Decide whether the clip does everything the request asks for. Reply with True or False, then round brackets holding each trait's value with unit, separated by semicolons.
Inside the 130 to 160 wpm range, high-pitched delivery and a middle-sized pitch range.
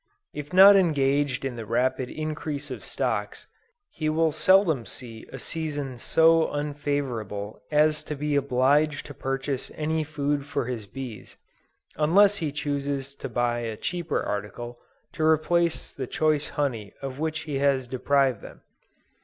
False (145 wpm; 145 Hz; 3.2 semitones)